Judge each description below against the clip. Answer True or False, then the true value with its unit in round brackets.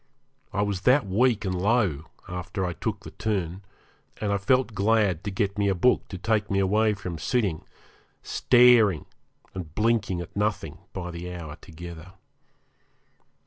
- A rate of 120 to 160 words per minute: True (150 wpm)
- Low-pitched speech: True (100 Hz)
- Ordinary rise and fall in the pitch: True (3.5 semitones)